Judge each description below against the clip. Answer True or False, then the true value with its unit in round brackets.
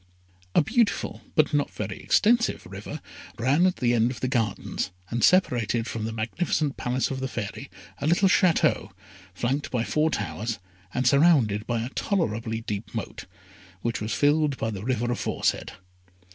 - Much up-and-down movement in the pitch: False (5.0 semitones)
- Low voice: True (125 Hz)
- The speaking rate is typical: True (160 wpm)